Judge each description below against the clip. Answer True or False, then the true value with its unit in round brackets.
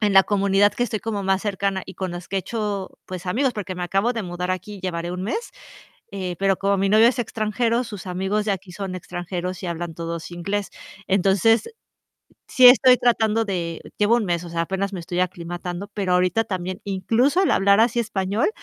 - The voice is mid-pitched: False (195 Hz)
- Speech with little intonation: False (3.0 semitones)